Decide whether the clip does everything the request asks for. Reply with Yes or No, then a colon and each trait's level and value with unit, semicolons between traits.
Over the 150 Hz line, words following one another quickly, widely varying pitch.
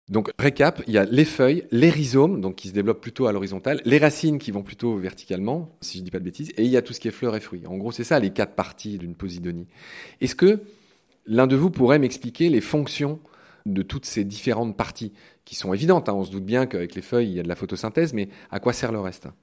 No: low, 115 Hz; fast, 265 wpm; wide, 6.6 semitones